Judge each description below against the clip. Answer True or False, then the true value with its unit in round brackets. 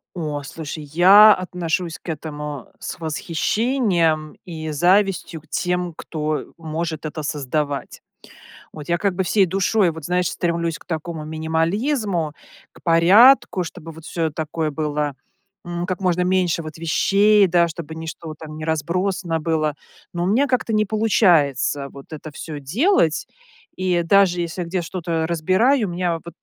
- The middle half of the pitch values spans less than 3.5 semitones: True (2.8 semitones)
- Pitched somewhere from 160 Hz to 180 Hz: True (170 Hz)